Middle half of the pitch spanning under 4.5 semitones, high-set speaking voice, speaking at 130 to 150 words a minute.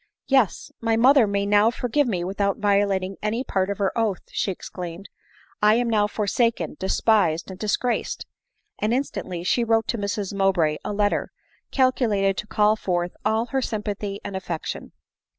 No: average, 2.9 semitones; high, 205 Hz; average, 180 wpm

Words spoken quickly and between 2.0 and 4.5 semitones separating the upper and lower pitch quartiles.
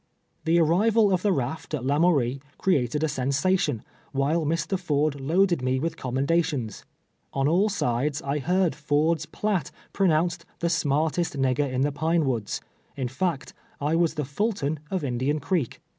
No: average, 175 wpm; average, 4.0 semitones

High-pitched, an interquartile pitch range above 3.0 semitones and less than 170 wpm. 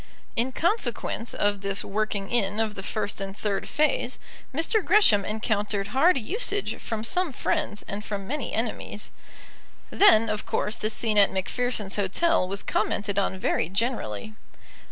Yes: high, 215 Hz; average, 4.4 semitones; average, 150 wpm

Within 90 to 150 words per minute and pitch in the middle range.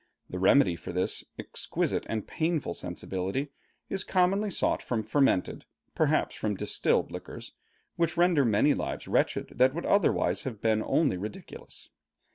No: average, 140 wpm; low, 130 Hz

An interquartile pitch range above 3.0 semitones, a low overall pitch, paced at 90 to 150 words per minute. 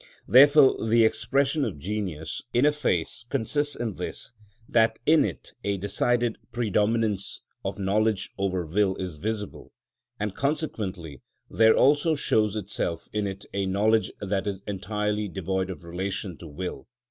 Yes: average, 3.4 semitones; low, 105 Hz; average, 145 wpm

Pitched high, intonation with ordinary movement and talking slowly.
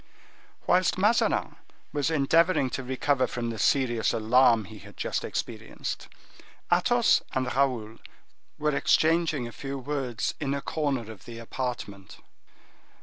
No: low, 130 Hz; average, 4.0 semitones; slow, 130 wpm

